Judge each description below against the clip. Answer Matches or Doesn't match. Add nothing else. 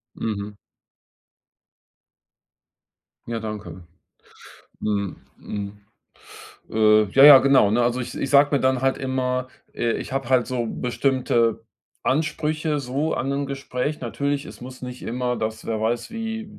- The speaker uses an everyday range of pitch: Matches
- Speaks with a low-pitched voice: Matches